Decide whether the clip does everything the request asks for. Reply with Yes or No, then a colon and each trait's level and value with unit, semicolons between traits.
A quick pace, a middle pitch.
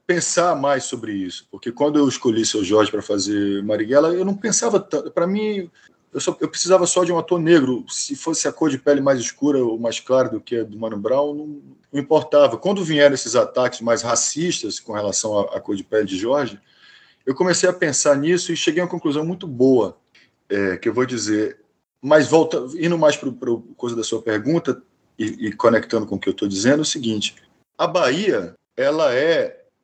Yes: fast, 210 wpm; medium, 145 Hz